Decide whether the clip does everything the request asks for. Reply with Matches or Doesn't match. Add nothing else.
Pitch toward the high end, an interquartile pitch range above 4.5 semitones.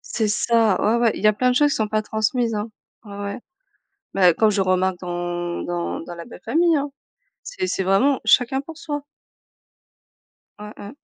Matches